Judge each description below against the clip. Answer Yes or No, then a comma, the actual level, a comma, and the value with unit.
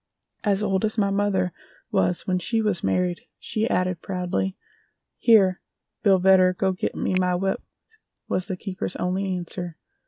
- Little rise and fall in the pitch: Yes, narrow, 1.6 semitones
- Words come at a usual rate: Yes, average, 155 wpm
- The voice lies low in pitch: No, medium, 185 Hz